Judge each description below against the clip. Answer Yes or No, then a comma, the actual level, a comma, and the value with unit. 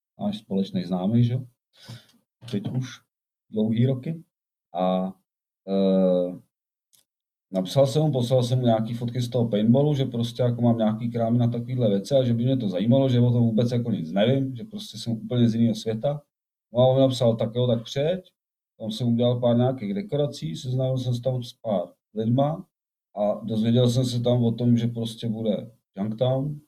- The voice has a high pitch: No, low, 120 Hz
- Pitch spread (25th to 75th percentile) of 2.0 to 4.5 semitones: Yes, average, 2.7 semitones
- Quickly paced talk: Yes, fast, 180 wpm